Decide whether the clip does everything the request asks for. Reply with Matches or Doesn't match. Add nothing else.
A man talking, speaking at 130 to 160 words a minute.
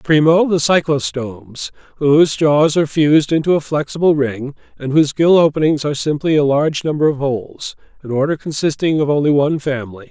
Doesn't match